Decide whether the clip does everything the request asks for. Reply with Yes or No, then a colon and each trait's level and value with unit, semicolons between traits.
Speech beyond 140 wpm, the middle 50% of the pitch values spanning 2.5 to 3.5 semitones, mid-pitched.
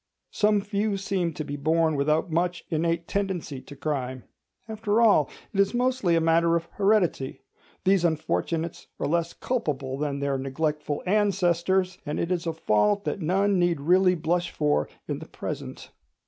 No: average, 160 wpm; average, 4.3 semitones; medium, 170 Hz